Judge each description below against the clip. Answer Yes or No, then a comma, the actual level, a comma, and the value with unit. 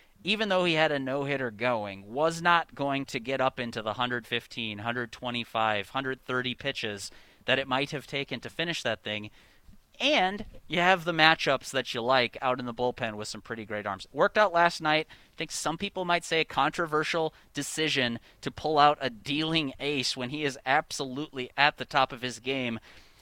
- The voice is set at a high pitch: No, low, 135 Hz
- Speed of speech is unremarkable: Yes, average, 190 wpm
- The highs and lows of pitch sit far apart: No, average, 4.2 semitones